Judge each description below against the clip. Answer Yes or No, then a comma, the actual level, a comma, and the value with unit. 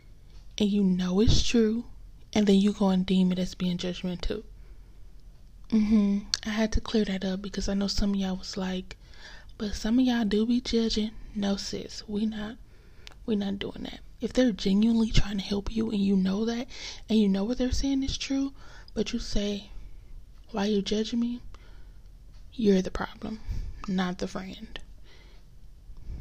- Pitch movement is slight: Yes, narrow, 2.3 semitones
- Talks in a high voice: Yes, high, 210 Hz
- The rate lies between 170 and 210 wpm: Yes, average, 180 wpm